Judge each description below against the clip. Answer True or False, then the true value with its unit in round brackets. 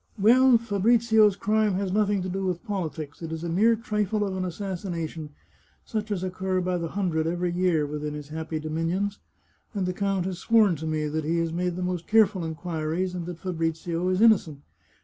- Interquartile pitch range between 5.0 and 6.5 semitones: False (3.7 semitones)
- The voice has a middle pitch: True (180 Hz)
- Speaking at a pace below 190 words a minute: False (195 wpm)